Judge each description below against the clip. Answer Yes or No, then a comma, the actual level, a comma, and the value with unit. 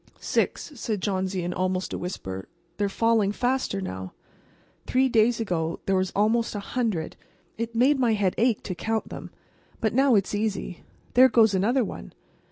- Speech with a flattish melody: No, average, 3.8 semitones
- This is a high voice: Yes, high, 210 Hz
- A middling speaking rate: Yes, average, 170 wpm